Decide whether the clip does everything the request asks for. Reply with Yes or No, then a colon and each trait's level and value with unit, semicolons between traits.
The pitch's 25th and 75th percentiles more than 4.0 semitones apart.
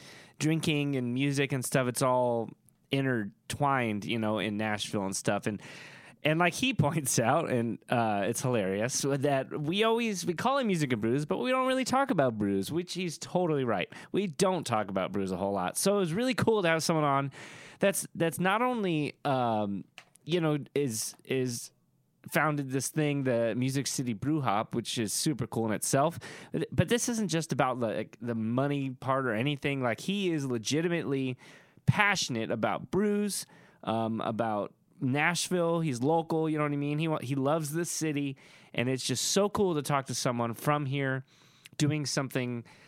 Yes: average, 5.1 semitones